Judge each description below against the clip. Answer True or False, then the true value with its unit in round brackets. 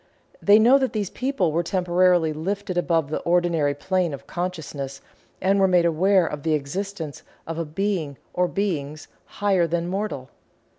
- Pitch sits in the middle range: True (175 Hz)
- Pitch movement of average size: True (3.8 semitones)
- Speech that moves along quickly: False (160 wpm)